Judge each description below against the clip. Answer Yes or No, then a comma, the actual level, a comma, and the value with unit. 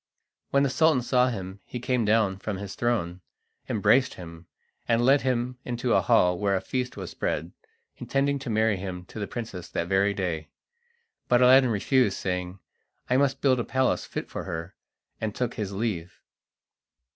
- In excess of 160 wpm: Yes, average, 175 wpm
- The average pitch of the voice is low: Yes, low, 110 Hz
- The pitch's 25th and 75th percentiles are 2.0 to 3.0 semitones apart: No, average, 5.1 semitones